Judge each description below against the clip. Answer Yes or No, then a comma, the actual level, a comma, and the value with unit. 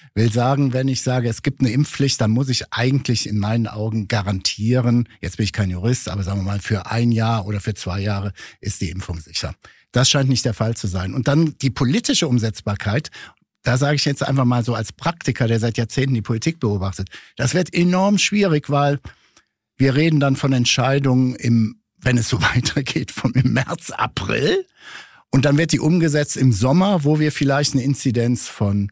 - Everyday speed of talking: No, fast, 200 wpm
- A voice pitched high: No, low, 125 Hz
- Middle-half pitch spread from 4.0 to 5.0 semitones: Yes, average, 4.3 semitones